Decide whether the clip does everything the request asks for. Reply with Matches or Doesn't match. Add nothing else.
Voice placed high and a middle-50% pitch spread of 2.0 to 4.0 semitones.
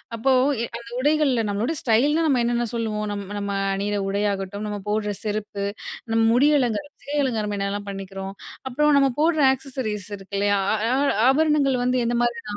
Doesn't match